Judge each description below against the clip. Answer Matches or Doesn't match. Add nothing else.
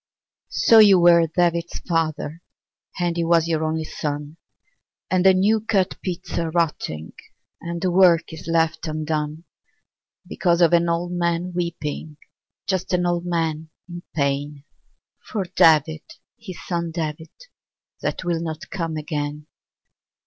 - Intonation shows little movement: Matches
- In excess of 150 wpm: Doesn't match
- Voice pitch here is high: Doesn't match